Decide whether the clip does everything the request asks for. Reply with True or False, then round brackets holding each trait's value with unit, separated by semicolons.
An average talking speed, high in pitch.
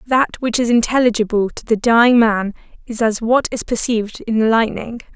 True (185 wpm; 230 Hz)